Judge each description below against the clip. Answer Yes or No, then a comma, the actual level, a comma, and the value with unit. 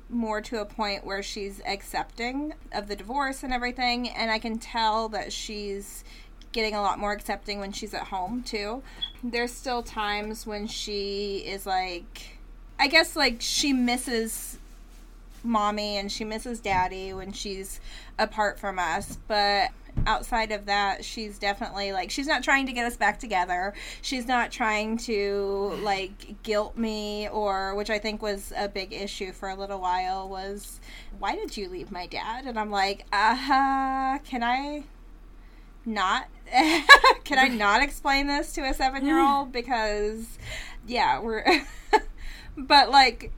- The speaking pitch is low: No, high, 215 Hz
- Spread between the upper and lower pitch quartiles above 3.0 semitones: Yes, average, 3.9 semitones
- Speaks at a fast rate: No, average, 155 wpm